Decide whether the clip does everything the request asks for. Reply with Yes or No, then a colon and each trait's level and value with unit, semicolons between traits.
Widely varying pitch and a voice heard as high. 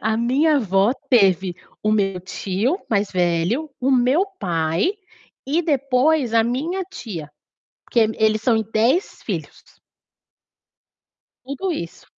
Yes: wide, 6.2 semitones; high, 230 Hz